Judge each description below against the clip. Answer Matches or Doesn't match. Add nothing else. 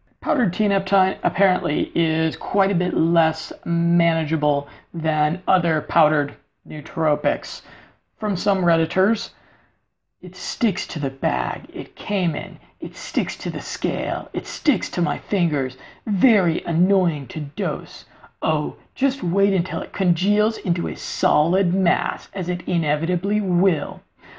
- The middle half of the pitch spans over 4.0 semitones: Doesn't match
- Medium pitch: Matches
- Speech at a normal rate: Doesn't match